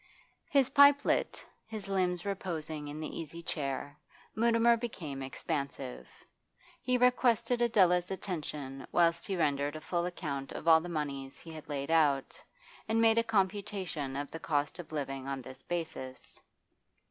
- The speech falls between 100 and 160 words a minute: Yes, average, 150 wpm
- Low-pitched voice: No, medium, 165 Hz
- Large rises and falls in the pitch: Yes, wide, 6.1 semitones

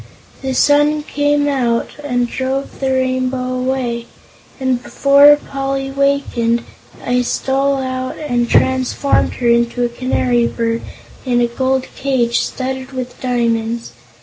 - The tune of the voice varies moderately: No, narrow, 2.1 semitones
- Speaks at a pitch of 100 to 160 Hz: No, very high, 260 Hz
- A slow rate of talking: Yes, slow, 125 wpm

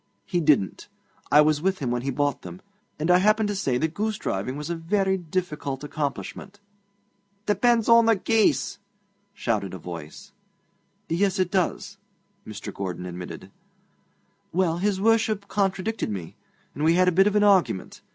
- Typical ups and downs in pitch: No, wide, 6.6 semitones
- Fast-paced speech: No, average, 160 wpm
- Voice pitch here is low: No, medium, 175 Hz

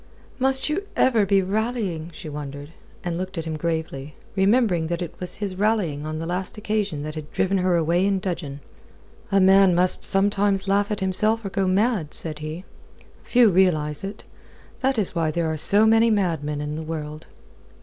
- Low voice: No, medium, 185 Hz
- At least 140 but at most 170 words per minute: No, average, 180 wpm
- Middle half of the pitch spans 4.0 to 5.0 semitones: Yes, average, 4.3 semitones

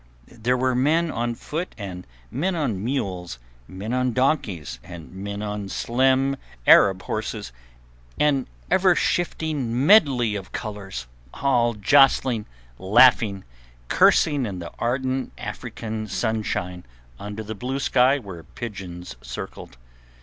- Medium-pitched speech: No, low, 115 Hz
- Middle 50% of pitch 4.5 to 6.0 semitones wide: Yes, average, 5.2 semitones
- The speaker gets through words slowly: Yes, slow, 120 wpm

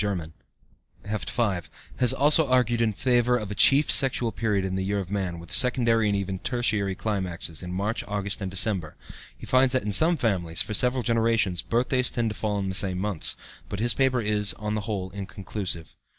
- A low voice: Yes, low, 105 Hz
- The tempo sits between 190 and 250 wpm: Yes, average, 200 wpm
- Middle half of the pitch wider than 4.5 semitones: No, average, 3.8 semitones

